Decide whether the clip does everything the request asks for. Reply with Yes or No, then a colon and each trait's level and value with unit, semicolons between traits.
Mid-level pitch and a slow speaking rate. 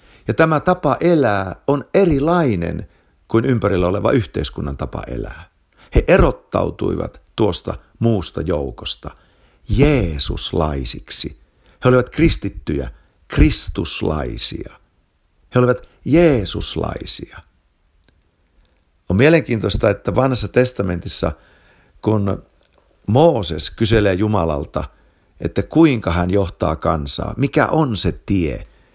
No: low, 100 Hz; slow, 90 wpm